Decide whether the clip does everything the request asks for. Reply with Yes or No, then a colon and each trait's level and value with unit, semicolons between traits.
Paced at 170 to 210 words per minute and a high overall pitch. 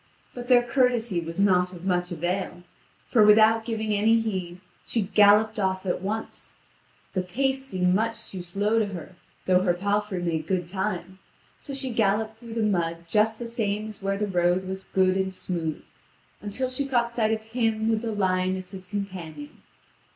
Yes: average, 180 wpm; high, 200 Hz